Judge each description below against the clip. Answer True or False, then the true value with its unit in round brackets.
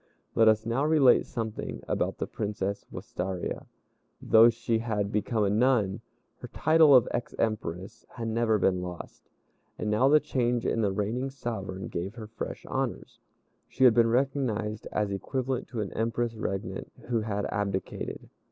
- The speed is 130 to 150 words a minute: False (160 wpm)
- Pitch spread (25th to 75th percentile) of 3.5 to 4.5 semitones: False (2.9 semitones)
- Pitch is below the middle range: True (110 Hz)